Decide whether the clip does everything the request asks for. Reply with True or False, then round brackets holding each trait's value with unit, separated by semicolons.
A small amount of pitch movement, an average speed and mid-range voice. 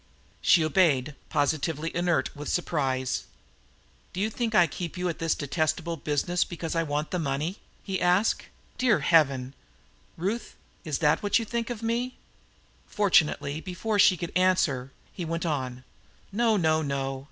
False (4.4 semitones; 150 wpm; 165 Hz)